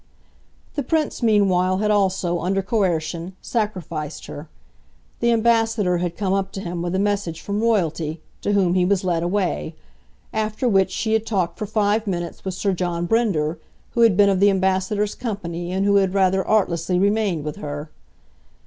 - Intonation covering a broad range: No, average, 3.2 semitones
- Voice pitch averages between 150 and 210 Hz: Yes, high, 190 Hz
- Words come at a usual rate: Yes, average, 175 wpm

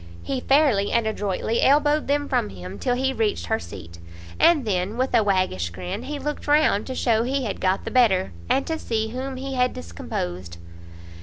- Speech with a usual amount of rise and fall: No, wide, 7.0 semitones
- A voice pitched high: Yes, high, 225 Hz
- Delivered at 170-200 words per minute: Yes, average, 190 wpm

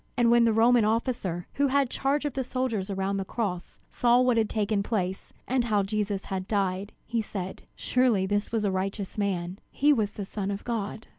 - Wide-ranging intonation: No, average, 3.4 semitones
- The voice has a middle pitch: No, high, 215 Hz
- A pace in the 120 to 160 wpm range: No, average, 200 wpm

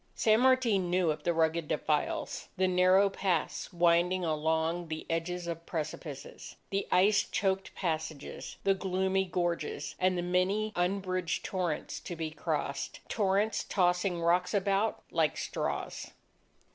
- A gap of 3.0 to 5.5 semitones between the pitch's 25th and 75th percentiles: No, narrow, 2.6 semitones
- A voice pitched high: No, medium, 180 Hz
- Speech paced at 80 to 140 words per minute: Yes, slow, 135 wpm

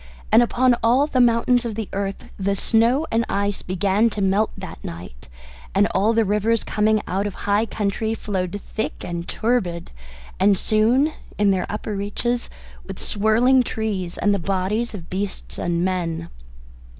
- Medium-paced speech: Yes, average, 160 wpm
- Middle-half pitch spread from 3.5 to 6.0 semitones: No, average, 3.1 semitones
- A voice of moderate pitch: No, high, 205 Hz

